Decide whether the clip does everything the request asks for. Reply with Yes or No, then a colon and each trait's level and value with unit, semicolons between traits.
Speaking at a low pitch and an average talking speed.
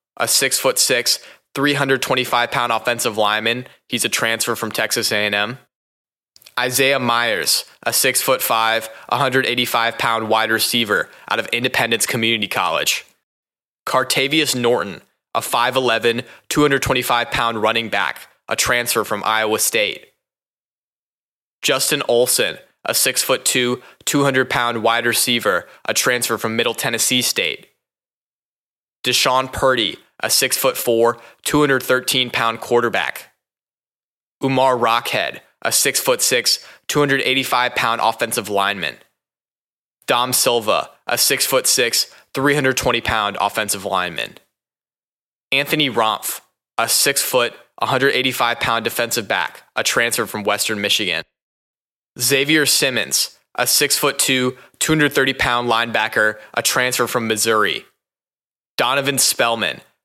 No: low, 120 Hz; slow, 120 wpm